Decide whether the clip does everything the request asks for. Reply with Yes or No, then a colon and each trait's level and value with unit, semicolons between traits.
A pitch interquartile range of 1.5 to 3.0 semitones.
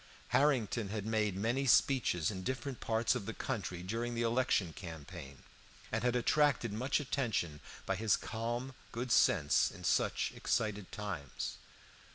No: average, 4.4 semitones